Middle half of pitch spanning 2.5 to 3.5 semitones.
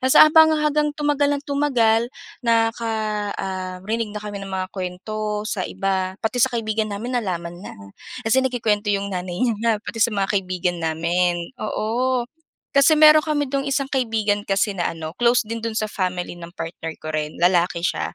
No: average, 5.1 semitones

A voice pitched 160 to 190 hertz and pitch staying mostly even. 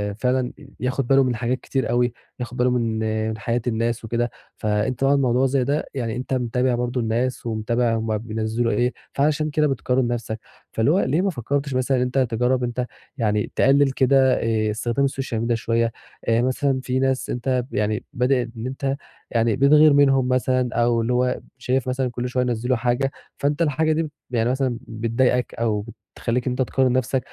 No: low, 125 Hz; narrow, 2.2 semitones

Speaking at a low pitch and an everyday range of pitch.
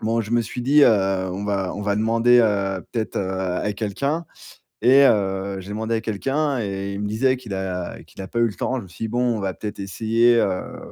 Yes: low, 110 Hz; average, 3.4 semitones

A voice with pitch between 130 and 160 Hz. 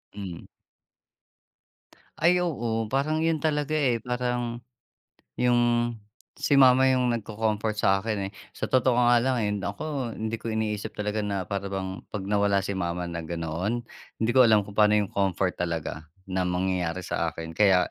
No: low, 105 Hz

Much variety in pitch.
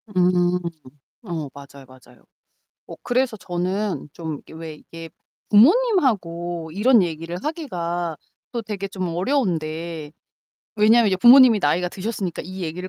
No: average, 4.6 semitones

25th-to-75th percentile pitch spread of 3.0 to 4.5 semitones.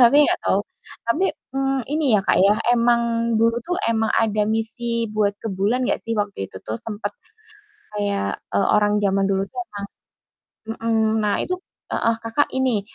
No: narrow, 2.4 semitones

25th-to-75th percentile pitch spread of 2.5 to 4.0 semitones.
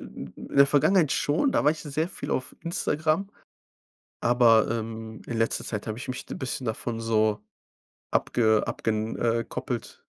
No: average, 4.6 semitones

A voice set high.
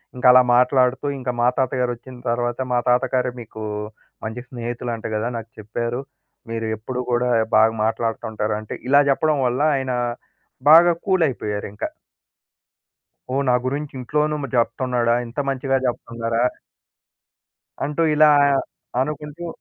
No: low, 125 Hz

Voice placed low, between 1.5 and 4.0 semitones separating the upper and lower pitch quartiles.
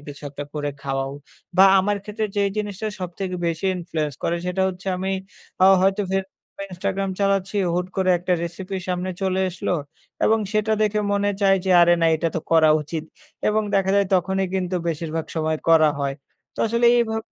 No: medium, 185 Hz; average, 3.1 semitones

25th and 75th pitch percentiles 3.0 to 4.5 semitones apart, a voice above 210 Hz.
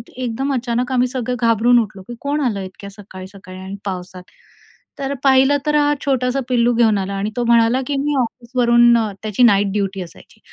Yes: average, 4.2 semitones; high, 235 Hz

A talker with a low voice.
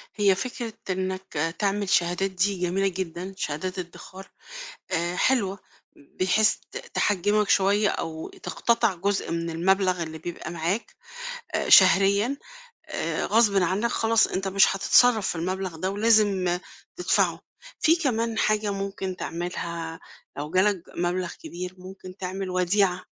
No: high, 190 Hz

